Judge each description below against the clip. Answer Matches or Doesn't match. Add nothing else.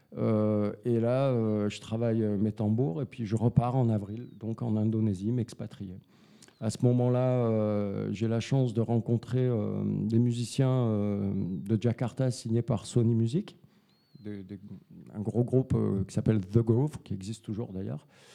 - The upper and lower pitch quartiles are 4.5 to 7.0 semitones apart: Doesn't match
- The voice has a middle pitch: Doesn't match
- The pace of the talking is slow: Doesn't match